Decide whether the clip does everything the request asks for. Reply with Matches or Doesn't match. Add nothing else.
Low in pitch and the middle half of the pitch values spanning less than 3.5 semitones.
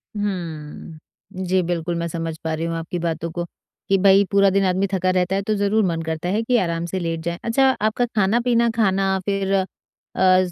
Doesn't match